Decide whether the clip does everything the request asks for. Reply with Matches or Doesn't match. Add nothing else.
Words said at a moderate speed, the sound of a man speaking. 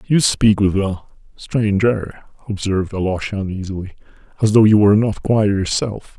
Matches